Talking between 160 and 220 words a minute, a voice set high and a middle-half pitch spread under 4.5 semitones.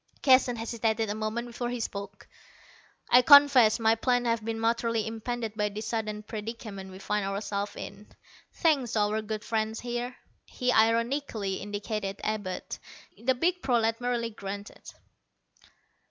No: average, 140 wpm; high, 225 Hz; narrow, 2.4 semitones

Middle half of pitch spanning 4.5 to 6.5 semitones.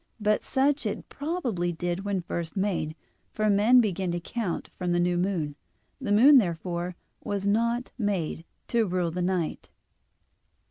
No: average, 4.0 semitones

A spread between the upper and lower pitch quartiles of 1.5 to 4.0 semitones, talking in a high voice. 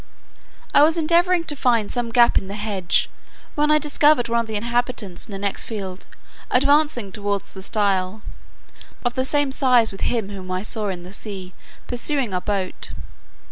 No: average, 5.2 semitones; high, 225 Hz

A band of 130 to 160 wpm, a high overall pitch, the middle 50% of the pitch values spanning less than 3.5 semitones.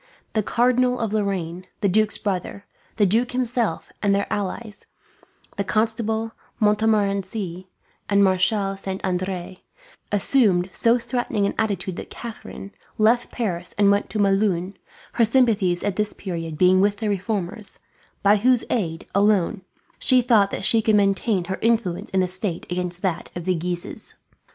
Yes: average, 150 wpm; high, 200 Hz; average, 3.0 semitones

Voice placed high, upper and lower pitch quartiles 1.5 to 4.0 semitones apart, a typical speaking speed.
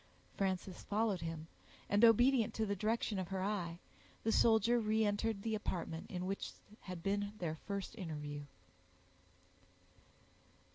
No: high, 200 Hz; average, 3.5 semitones; slow, 130 wpm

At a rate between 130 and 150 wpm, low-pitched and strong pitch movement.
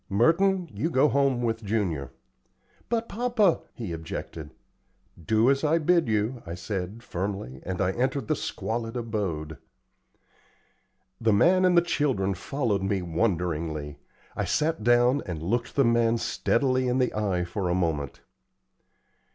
Yes: average, 145 wpm; low, 115 Hz; wide, 7.1 semitones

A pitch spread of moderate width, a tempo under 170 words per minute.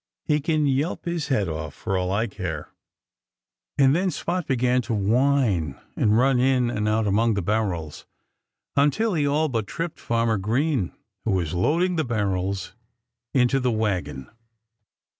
No: wide, 6.2 semitones; average, 155 wpm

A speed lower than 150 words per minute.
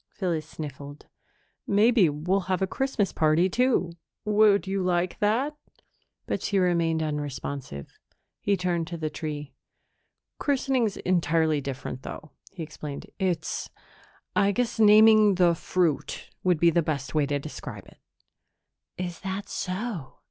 Yes: slow, 135 wpm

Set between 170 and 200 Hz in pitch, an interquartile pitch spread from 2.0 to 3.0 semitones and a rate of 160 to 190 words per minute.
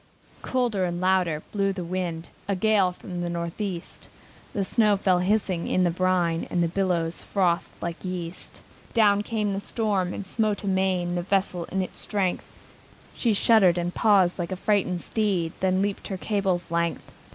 Yes: medium, 185 Hz; narrow, 2.5 semitones; average, 170 wpm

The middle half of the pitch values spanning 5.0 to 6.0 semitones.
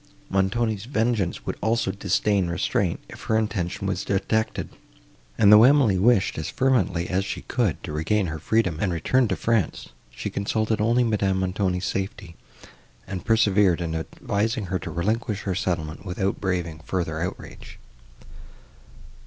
No: average, 3.5 semitones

